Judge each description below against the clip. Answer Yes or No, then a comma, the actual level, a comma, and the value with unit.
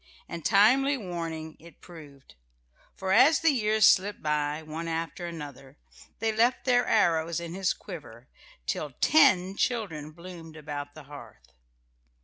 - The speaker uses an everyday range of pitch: No, wide, 5.7 semitones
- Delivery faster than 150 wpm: No, slow, 135 wpm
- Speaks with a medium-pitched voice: Yes, medium, 170 Hz